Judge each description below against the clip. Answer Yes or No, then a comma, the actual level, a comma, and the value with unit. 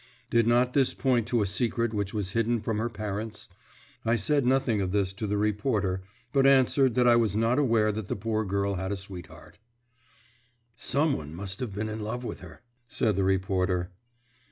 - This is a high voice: No, low, 110 Hz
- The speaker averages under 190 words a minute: No, average, 195 wpm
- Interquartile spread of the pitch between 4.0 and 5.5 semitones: No, average, 3.3 semitones